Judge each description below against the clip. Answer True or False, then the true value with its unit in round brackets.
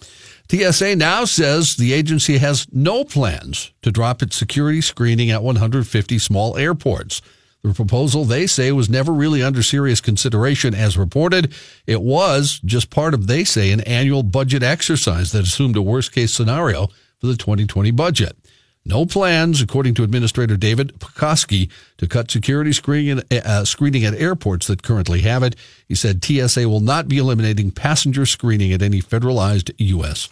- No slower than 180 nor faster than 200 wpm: False (160 wpm)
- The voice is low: True (125 Hz)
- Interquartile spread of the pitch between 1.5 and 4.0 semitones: False (4.7 semitones)